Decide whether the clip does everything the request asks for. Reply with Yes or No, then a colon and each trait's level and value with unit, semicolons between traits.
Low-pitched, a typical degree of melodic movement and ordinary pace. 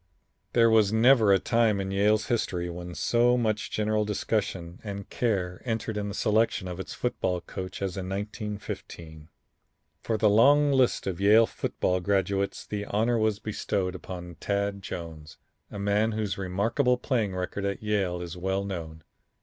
Yes: low, 100 Hz; average, 3.0 semitones; average, 160 wpm